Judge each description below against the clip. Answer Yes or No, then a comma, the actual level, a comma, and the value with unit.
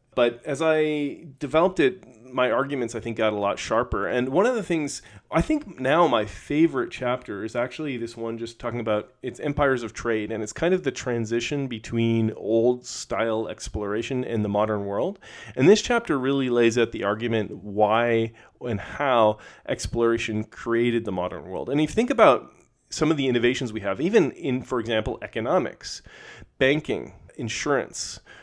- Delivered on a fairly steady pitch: No, average, 3.8 semitones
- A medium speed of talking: Yes, average, 175 wpm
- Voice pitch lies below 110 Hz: No, low, 120 Hz